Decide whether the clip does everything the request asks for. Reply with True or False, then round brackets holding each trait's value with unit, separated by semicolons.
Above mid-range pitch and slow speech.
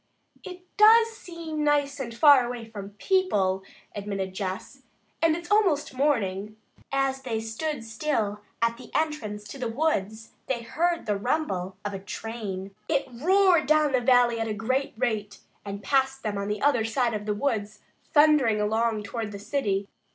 False (235 Hz; 165 wpm)